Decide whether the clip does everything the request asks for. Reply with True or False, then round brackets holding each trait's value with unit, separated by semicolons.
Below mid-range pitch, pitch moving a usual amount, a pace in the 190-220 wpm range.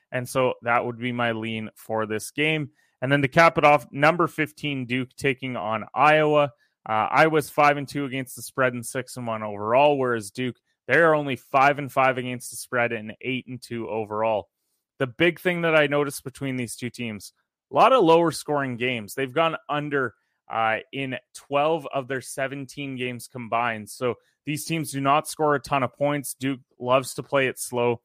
True (130 Hz; 3.4 semitones; 200 wpm)